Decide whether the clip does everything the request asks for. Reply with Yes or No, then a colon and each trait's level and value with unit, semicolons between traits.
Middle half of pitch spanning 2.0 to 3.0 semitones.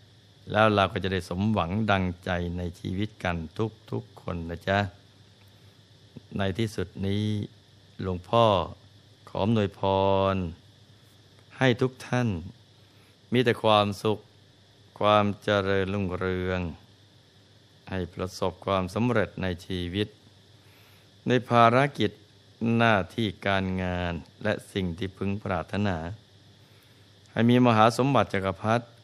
Yes: narrow, 2.4 semitones